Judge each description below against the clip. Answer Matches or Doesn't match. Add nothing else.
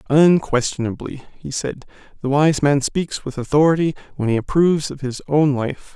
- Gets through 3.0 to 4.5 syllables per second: Doesn't match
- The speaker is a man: Matches